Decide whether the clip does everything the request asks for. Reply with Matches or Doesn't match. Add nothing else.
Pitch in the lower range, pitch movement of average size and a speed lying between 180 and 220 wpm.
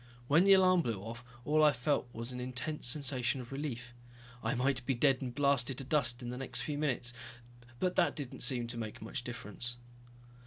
Matches